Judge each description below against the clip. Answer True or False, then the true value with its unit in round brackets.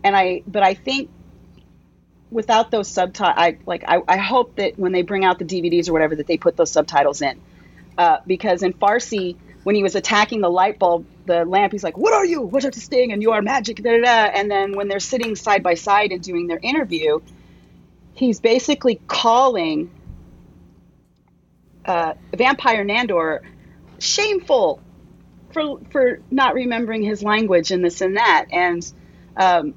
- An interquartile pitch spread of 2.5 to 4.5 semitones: False (5.2 semitones)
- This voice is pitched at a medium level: False (200 Hz)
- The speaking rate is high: False (175 wpm)